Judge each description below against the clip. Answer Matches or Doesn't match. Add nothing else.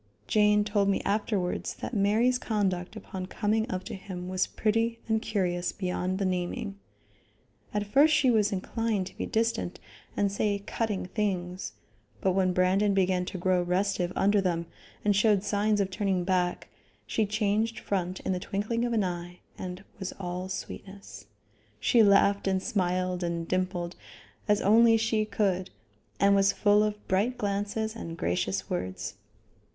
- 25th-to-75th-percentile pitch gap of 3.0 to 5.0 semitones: Doesn't match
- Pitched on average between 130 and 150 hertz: Doesn't match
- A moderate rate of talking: Matches